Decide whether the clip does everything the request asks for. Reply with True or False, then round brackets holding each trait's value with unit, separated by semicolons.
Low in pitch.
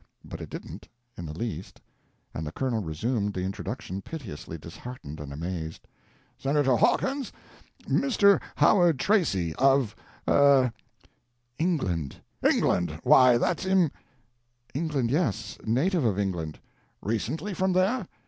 True (120 Hz)